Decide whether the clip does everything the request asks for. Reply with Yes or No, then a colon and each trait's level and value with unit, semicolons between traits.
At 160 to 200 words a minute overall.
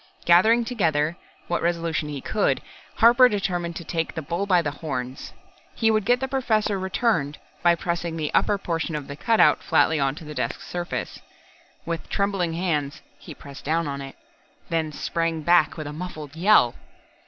Yes: average, 170 wpm